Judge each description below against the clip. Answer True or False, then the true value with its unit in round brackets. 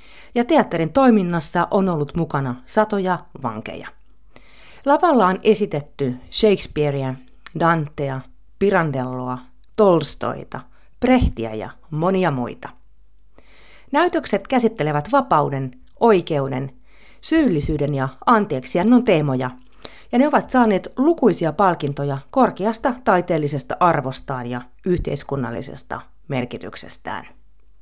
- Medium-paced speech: False (85 wpm)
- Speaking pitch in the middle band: True (160 Hz)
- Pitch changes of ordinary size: False (8.2 semitones)